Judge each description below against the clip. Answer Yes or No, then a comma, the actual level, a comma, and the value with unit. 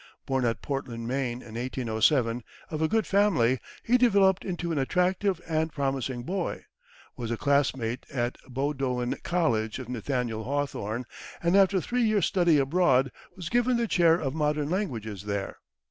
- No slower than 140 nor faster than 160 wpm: Yes, average, 155 wpm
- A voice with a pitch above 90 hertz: Yes, medium, 140 Hz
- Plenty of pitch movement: Yes, wide, 6.5 semitones